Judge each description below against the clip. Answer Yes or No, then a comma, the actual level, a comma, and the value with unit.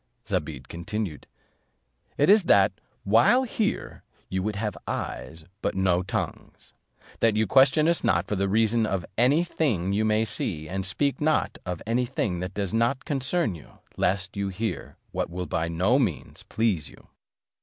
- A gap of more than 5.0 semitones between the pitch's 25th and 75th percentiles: Yes, wide, 5.4 semitones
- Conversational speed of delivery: Yes, average, 165 wpm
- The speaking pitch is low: Yes, low, 105 Hz